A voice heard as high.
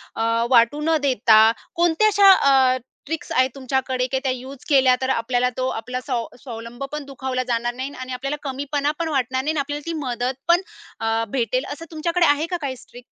Yes: very high, 265 Hz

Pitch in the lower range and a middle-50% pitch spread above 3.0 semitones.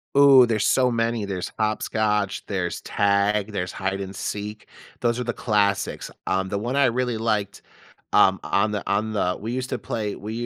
No: low, 105 Hz; average, 2.7 semitones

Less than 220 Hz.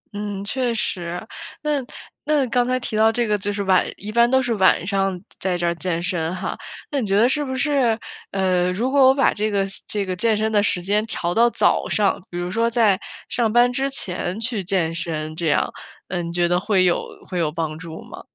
Yes: high, 200 Hz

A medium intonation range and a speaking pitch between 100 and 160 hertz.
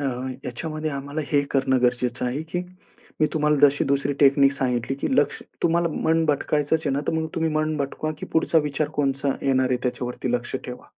Yes: average, 3.0 semitones; medium, 140 Hz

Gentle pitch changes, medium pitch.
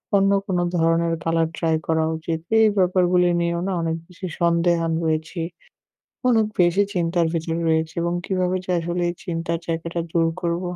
Yes: narrow, 1.4 semitones; medium, 170 Hz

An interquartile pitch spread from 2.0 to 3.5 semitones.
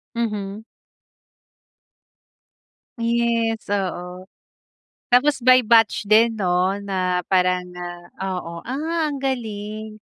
No: average, 4.1 semitones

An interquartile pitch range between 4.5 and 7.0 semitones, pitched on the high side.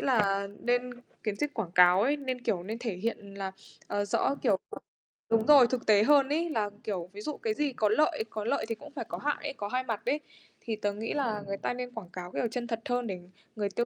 No: average, 3.9 semitones; high, 225 Hz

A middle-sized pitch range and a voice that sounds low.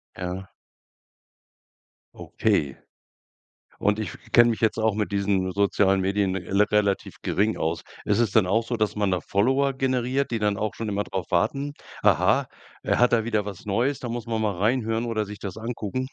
Yes: average, 3.0 semitones; low, 105 Hz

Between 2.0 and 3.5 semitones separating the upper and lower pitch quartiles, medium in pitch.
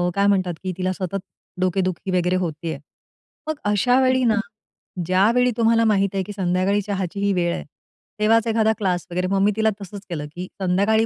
No: average, 3.1 semitones; high, 195 Hz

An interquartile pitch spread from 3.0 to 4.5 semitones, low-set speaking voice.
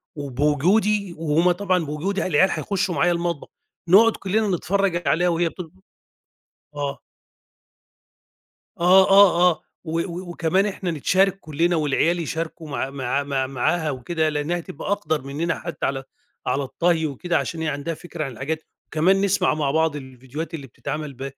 No: average, 3.7 semitones; medium, 165 Hz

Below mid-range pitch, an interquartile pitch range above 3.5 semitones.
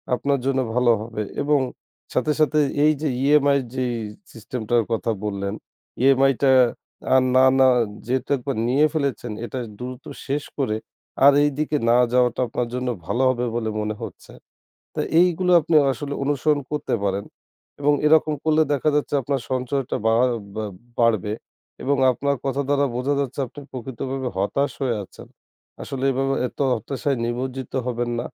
No: low, 130 Hz; average, 2.9 semitones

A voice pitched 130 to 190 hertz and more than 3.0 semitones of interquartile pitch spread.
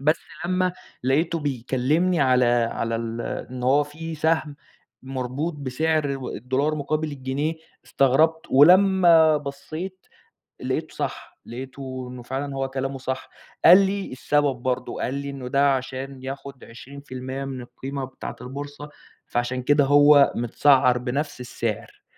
No: medium, 140 Hz; average, 2.7 semitones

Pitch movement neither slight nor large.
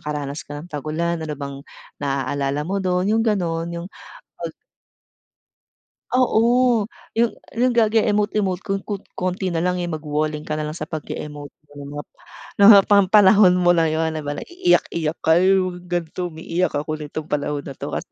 Yes: average, 4.6 semitones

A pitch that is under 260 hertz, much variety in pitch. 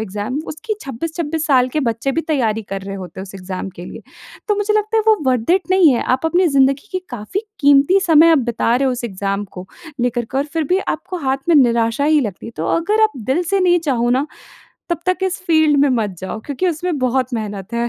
No: very high, 270 Hz; wide, 6.6 semitones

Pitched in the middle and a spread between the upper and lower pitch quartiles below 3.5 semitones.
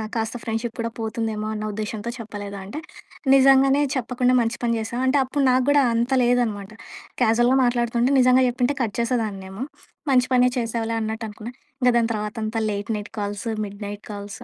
No: high, 230 Hz; average, 2.7 semitones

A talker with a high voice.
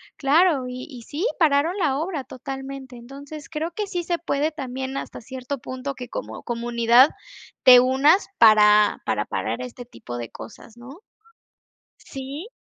Yes: very high, 270 Hz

